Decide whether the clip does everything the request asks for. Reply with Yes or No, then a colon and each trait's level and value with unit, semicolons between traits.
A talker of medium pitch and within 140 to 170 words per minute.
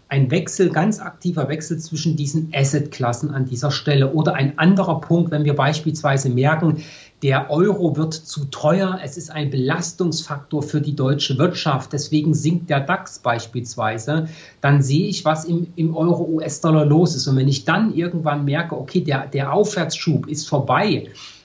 Yes: medium, 155 Hz; average, 160 wpm